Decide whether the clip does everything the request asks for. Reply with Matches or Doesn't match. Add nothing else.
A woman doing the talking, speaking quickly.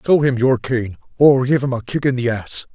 Doesn't match